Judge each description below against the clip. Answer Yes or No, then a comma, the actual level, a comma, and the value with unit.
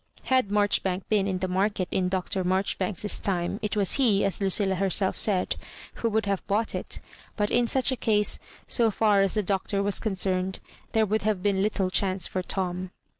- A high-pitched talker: Yes, high, 195 Hz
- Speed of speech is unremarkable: Yes, average, 190 wpm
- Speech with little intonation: Yes, narrow, 2.1 semitones